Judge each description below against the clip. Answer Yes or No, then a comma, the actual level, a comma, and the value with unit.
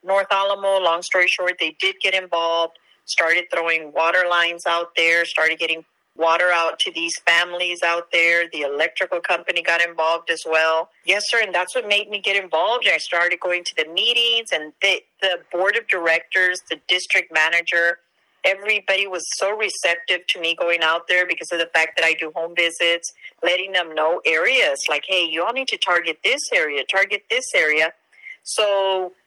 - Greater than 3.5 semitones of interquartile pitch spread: No, average, 2.8 semitones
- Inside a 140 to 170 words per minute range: No, average, 185 wpm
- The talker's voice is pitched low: No, medium, 175 Hz